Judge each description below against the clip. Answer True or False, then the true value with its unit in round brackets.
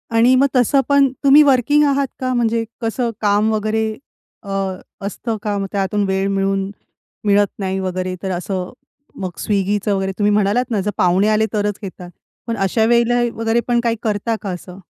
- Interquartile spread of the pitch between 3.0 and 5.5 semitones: True (3.3 semitones)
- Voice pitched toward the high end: True (210 Hz)